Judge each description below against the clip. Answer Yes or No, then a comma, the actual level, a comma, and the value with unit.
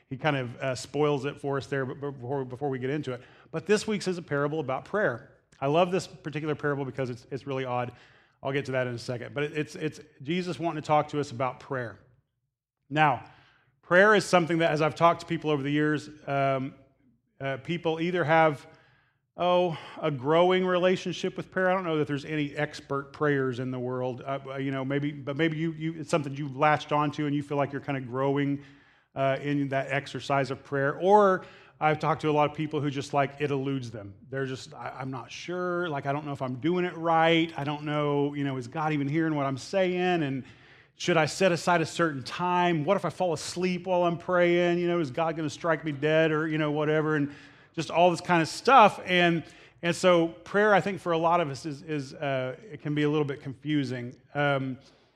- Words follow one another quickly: Yes, fast, 240 wpm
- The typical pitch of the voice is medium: Yes, medium, 150 Hz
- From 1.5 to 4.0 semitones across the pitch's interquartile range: Yes, average, 3.4 semitones